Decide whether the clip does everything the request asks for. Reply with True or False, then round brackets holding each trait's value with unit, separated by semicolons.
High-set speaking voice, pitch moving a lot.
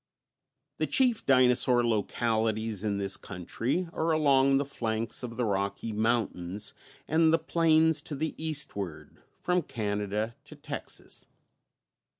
False (120 Hz; 6.6 semitones)